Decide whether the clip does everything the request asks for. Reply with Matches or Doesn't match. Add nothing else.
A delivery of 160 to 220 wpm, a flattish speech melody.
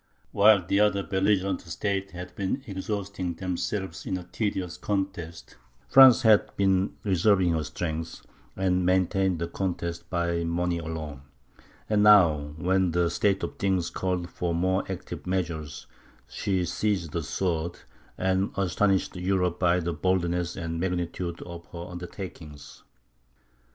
Doesn't match